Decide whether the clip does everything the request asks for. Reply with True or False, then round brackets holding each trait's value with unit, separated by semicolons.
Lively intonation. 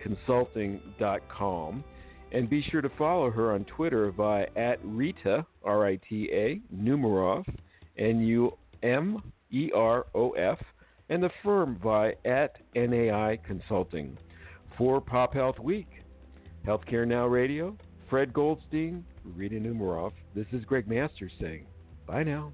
True (6.0 semitones)